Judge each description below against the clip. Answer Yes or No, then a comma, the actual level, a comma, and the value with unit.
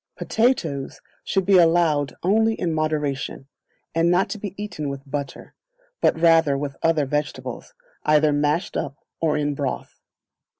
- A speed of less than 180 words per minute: Yes, average, 140 wpm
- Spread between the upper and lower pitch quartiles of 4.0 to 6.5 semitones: No, average, 3.5 semitones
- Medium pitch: Yes, medium, 155 Hz